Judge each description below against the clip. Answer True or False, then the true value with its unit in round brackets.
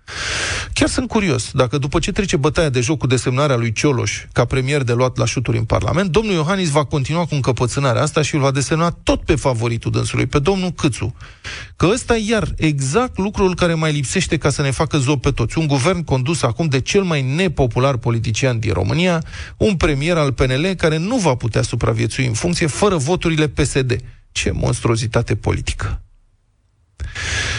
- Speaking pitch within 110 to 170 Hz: True (140 Hz)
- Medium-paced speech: False (185 wpm)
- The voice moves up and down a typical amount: False (6.0 semitones)